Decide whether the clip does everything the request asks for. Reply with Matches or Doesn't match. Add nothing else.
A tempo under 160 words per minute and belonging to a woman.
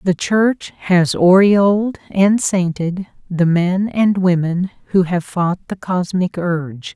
Matches